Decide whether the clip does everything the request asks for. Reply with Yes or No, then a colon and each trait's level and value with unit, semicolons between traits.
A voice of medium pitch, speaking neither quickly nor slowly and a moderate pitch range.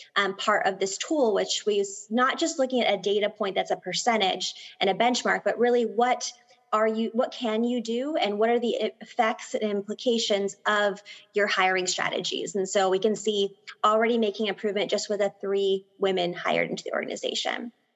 No: high, 210 Hz; average, 190 wpm; average, 3.2 semitones